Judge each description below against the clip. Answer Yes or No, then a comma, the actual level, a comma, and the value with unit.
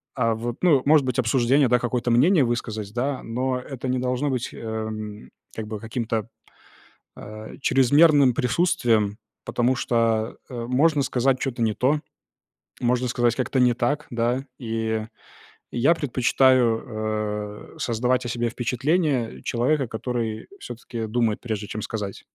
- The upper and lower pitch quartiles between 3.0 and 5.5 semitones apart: No, narrow, 2.6 semitones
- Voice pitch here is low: Yes, low, 120 Hz